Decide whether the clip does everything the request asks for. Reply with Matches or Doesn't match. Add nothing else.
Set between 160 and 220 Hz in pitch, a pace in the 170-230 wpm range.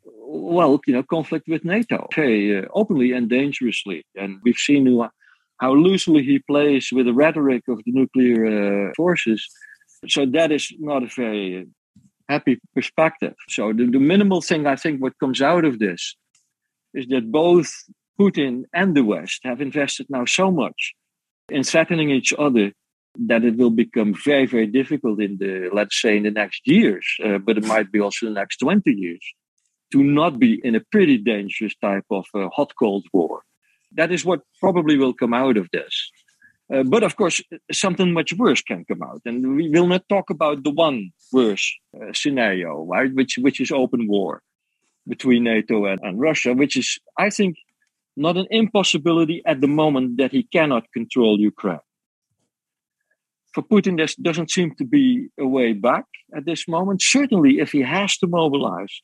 Doesn't match